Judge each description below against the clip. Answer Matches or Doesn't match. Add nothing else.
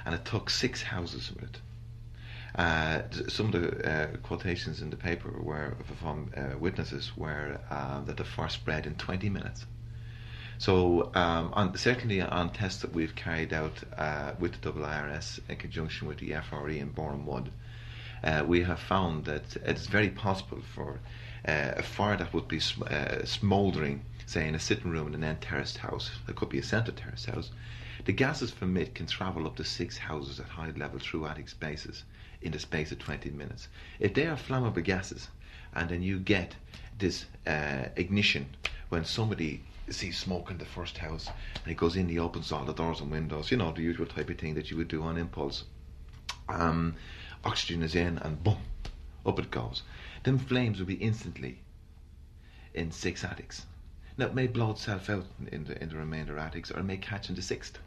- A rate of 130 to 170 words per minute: Doesn't match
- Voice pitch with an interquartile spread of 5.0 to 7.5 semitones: Matches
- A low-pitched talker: Matches